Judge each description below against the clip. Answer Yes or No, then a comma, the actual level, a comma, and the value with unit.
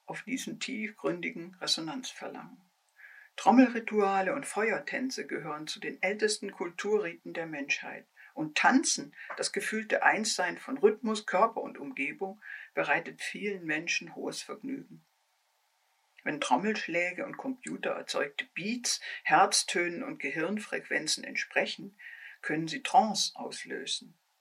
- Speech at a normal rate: No, slow, 105 wpm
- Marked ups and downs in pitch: Yes, wide, 5.9 semitones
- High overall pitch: Yes, high, 220 Hz